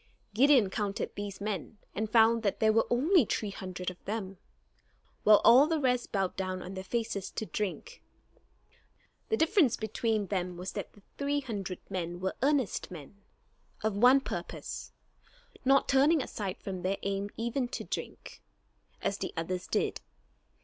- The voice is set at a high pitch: Yes, high, 215 Hz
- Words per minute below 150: No, average, 155 wpm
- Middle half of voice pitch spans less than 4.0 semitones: No, average, 4.6 semitones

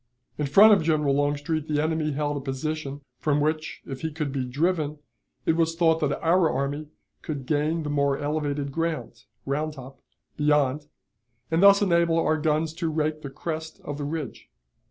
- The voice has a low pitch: No, medium, 150 Hz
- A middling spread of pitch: No, narrow, 2.0 semitones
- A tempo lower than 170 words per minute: No, average, 175 wpm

